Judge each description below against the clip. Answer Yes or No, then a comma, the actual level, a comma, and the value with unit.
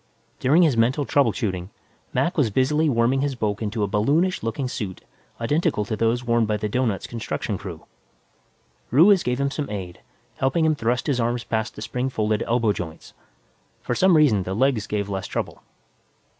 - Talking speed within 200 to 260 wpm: No, average, 180 wpm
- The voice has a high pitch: No, low, 120 Hz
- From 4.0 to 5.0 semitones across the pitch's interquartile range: Yes, average, 4.7 semitones